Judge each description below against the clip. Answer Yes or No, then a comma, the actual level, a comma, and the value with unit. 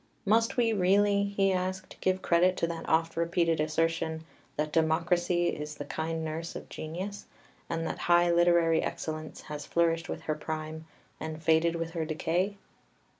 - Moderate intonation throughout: No, narrow, 2.2 semitones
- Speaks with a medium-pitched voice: Yes, medium, 165 Hz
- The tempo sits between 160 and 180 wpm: Yes, average, 165 wpm